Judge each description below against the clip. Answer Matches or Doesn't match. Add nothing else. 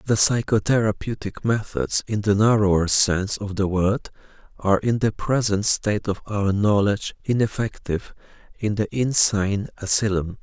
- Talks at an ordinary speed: Doesn't match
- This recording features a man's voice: Matches